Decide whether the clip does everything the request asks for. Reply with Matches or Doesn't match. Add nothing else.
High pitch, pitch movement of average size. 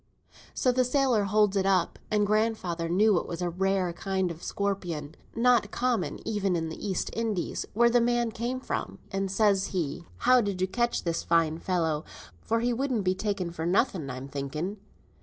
Matches